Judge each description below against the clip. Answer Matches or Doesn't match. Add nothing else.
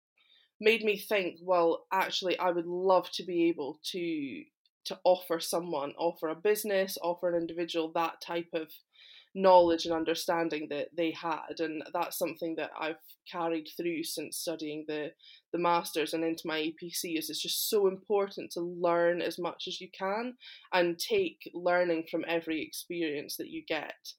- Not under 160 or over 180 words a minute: Matches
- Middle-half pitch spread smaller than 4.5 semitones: Matches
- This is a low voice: Doesn't match